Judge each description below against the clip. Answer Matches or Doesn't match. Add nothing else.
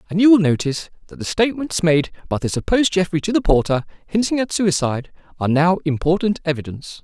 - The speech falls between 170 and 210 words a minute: Matches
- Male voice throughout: Matches